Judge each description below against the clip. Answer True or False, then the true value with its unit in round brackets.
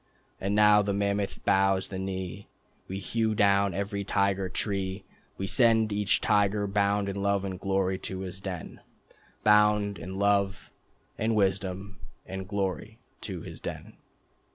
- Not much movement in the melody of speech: True (1.2 semitones)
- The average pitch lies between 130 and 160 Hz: False (100 Hz)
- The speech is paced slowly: False (145 wpm)